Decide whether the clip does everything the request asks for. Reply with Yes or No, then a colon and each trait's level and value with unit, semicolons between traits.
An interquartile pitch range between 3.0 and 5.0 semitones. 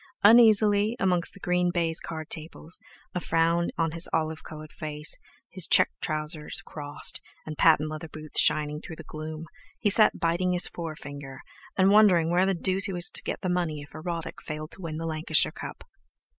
No: narrow, 2.5 semitones